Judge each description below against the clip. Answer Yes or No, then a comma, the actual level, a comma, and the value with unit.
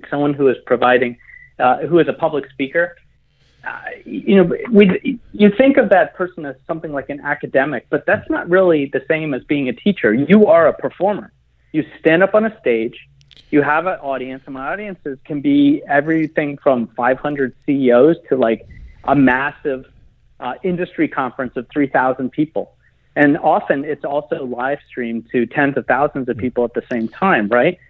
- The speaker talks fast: No, average, 180 wpm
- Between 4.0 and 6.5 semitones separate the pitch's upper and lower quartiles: Yes, average, 4.7 semitones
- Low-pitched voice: No, medium, 145 Hz